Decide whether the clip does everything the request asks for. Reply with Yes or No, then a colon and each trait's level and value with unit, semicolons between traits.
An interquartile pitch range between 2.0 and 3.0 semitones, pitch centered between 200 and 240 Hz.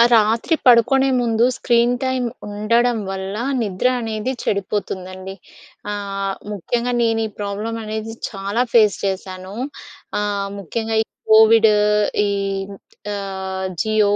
Yes: average, 2.7 semitones; high, 215 Hz